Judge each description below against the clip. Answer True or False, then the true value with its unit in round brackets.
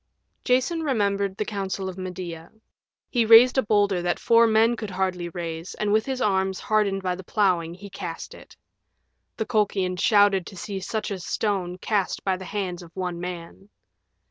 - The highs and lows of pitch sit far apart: False (2.8 semitones)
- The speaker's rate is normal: True (170 wpm)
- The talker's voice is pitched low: False (195 Hz)